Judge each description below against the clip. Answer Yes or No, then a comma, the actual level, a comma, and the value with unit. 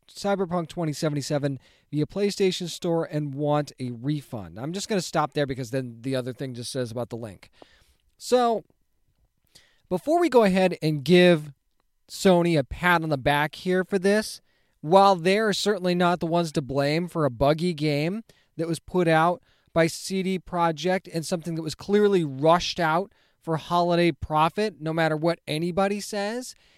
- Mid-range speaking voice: Yes, medium, 165 Hz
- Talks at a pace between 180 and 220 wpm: No, average, 170 wpm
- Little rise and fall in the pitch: No, average, 4.2 semitones